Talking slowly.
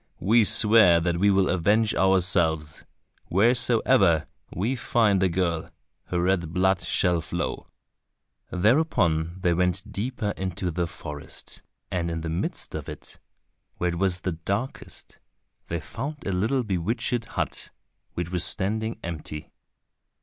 Yes: slow, 130 wpm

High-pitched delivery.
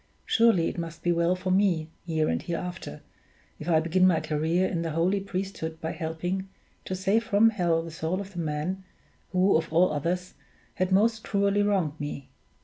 No: medium, 180 Hz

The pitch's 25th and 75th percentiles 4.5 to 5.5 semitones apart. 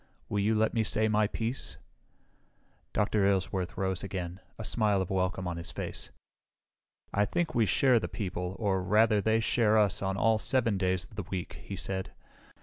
No: narrow, 2.6 semitones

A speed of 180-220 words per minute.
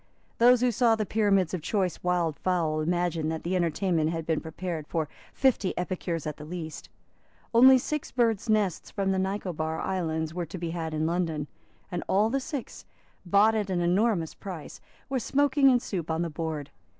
Yes: average, 185 wpm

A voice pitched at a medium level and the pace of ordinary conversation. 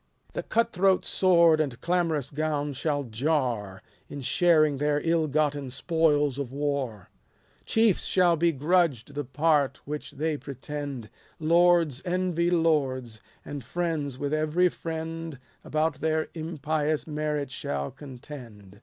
No: medium, 150 Hz; slow, 125 wpm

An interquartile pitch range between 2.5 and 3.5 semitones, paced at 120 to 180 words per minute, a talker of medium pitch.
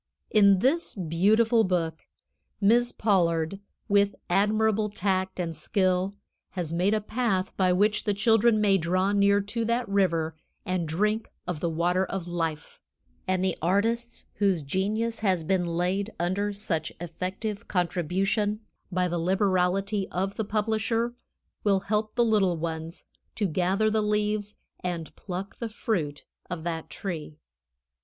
No: average, 3.1 semitones; average, 140 wpm; high, 195 Hz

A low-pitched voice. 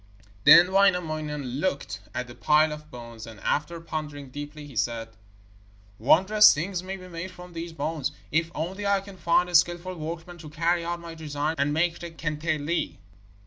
No: medium, 160 Hz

